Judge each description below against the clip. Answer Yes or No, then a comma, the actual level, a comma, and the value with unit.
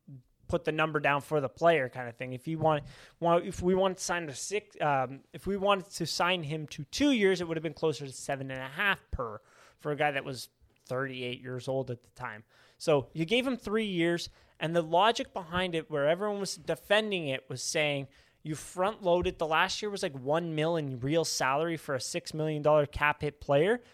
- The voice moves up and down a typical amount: Yes, average, 4.5 semitones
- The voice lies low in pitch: No, medium, 155 Hz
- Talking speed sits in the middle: No, fast, 230 wpm